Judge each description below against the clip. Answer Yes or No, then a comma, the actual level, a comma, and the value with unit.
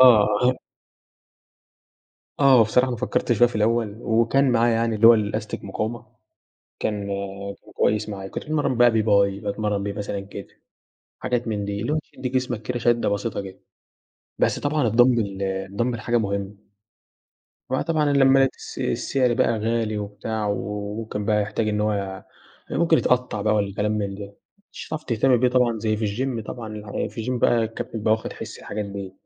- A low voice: Yes, low, 110 Hz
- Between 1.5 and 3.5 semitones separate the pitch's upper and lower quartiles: Yes, average, 3.0 semitones